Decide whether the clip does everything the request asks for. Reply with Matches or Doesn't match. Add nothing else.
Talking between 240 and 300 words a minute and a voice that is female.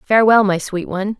Doesn't match